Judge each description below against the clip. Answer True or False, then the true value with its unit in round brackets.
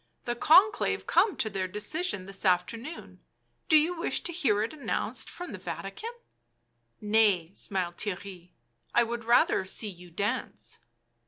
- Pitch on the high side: True (215 Hz)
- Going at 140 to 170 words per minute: True (160 wpm)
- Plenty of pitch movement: True (8.1 semitones)